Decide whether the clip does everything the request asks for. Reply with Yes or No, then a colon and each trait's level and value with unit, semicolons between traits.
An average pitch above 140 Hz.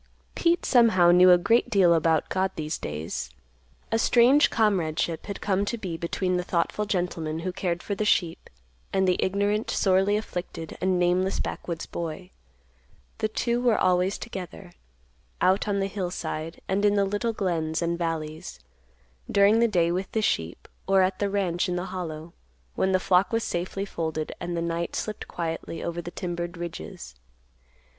Yes: medium, 185 Hz